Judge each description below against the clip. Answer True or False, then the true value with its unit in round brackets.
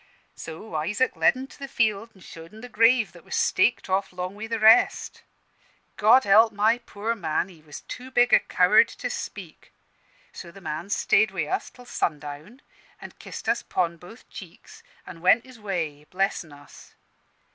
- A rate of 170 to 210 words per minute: True (180 wpm)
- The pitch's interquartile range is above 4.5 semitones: True (5.1 semitones)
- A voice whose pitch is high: True (200 Hz)